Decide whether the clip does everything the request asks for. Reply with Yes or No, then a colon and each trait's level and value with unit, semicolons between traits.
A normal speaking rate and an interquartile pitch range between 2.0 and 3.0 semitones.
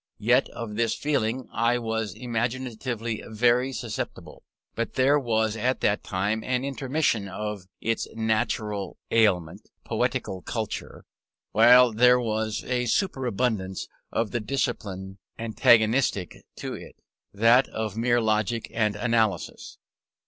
No: slow, 120 wpm; narrow, 2.5 semitones